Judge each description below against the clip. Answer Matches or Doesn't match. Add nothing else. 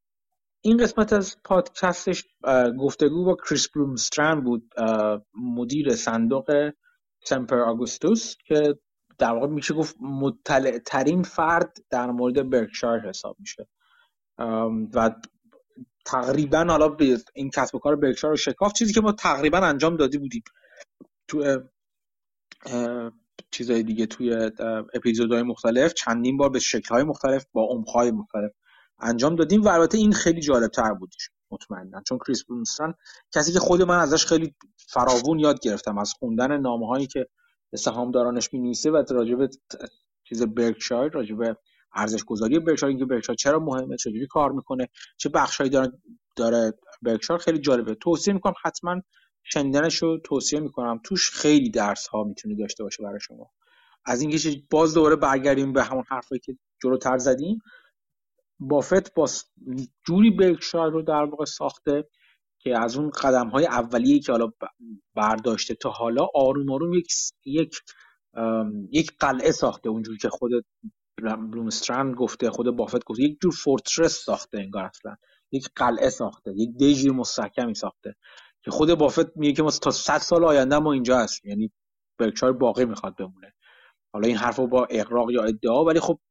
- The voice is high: Doesn't match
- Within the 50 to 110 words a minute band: Doesn't match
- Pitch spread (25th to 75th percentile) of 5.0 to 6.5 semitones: Matches